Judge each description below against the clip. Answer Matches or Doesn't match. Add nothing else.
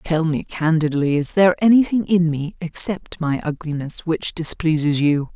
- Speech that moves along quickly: Doesn't match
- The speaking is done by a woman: Matches